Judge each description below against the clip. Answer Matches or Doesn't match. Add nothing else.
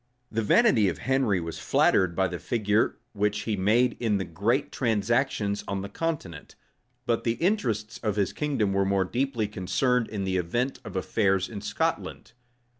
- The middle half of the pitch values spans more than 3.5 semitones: Matches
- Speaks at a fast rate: Doesn't match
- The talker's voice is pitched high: Doesn't match